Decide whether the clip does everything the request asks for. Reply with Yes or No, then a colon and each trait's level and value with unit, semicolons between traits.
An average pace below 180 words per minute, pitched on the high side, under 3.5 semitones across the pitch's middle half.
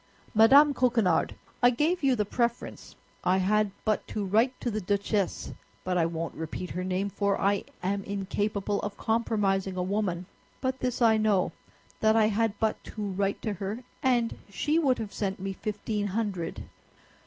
Yes: average, 165 wpm; high, 205 Hz; average, 2.8 semitones